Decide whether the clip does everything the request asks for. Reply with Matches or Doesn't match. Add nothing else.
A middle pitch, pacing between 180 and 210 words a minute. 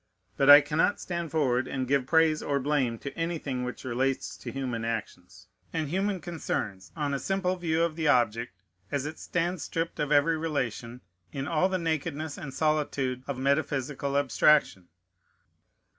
Doesn't match